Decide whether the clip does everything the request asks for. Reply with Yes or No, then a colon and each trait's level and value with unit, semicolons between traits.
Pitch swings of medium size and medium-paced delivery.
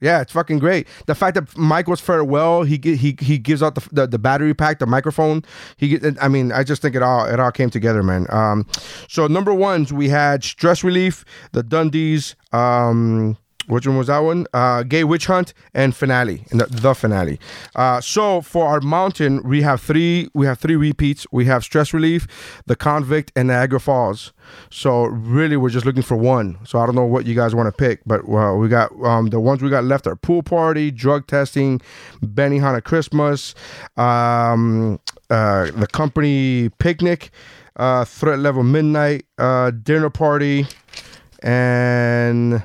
Yes: average, 4.2 semitones; average, 185 wpm